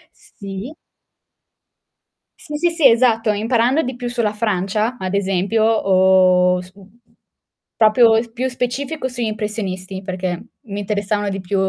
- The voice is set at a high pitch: Yes, high, 215 Hz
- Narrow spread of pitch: No, average, 3.7 semitones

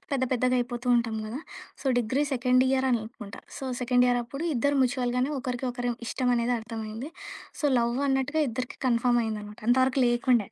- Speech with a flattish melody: Yes, narrow, 1.6 semitones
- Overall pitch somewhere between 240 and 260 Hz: Yes, high, 245 Hz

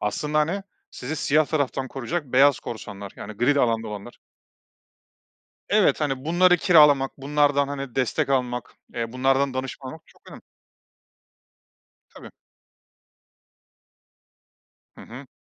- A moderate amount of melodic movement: Yes, average, 3.1 semitones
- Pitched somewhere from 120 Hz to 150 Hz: Yes, low, 135 Hz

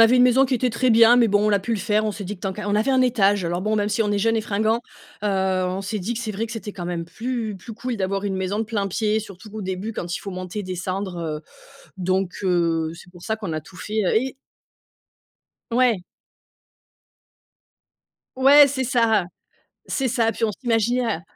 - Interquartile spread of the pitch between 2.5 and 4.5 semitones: Yes, average, 3.4 semitones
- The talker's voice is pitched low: No, high, 210 Hz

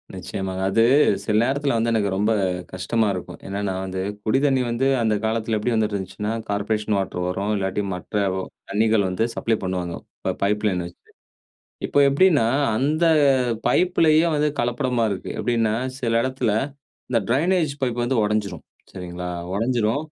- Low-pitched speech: Yes, low, 110 Hz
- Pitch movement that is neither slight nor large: Yes, average, 4.1 semitones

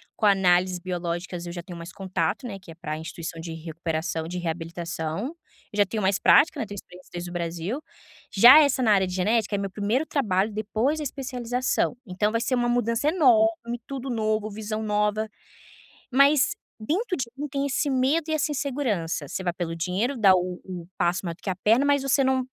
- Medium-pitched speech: No, high, 210 Hz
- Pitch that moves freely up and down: Yes, wide, 6.4 semitones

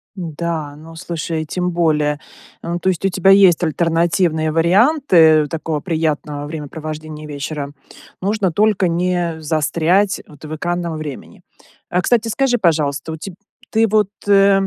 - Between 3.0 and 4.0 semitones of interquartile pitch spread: Yes, average, 3.3 semitones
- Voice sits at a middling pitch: Yes, medium, 165 Hz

